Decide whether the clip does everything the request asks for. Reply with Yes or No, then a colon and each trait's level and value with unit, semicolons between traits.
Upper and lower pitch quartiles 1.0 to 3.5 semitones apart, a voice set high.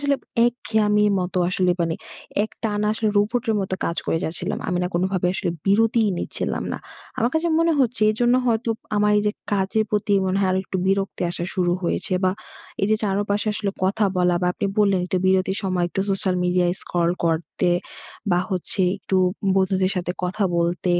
Yes: average, 2.8 semitones; high, 195 Hz